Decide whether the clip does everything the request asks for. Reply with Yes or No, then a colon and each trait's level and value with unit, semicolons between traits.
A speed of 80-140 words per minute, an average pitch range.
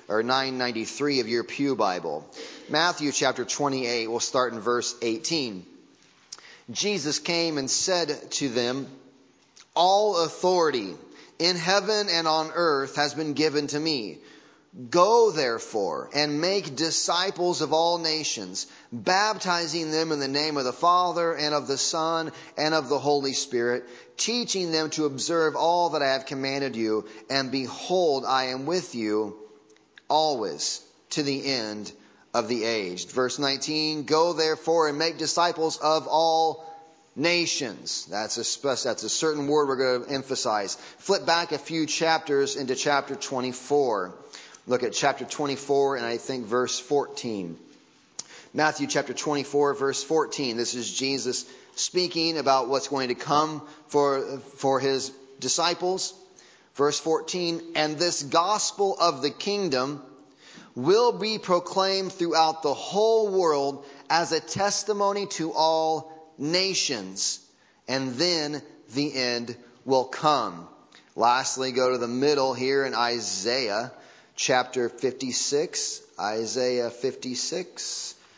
Yes: slow, 135 wpm; average, 4.0 semitones